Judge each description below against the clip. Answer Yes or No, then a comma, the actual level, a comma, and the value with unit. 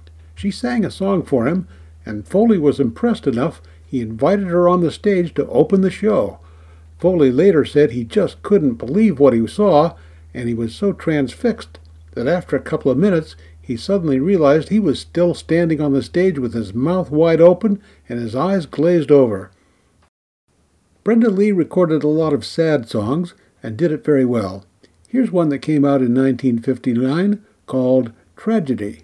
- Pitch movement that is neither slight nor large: No, wide, 7.9 semitones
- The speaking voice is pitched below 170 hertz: Yes, medium, 140 Hz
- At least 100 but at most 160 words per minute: No, average, 175 wpm